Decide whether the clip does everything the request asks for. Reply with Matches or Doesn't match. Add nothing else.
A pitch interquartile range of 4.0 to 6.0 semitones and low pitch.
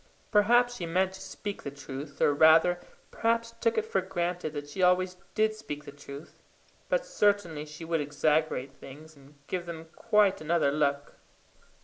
Doesn't match